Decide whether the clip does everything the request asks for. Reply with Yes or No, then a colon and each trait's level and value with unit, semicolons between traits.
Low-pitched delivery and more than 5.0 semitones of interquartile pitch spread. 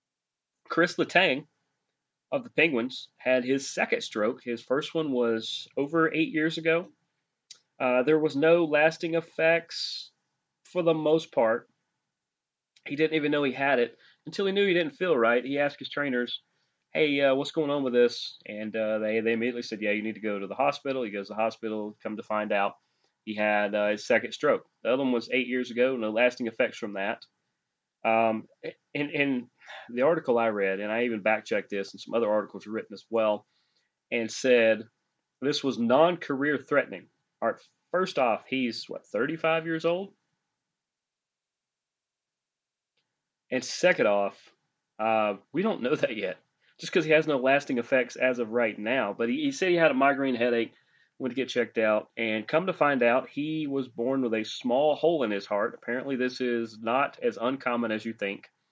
Yes: low, 125 Hz; wide, 5.4 semitones